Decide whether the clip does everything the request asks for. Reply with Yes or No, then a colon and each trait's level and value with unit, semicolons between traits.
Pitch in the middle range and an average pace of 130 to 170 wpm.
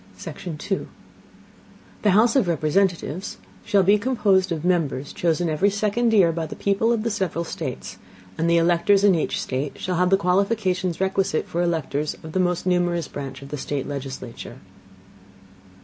Yes: medium, 175 Hz; average, 165 wpm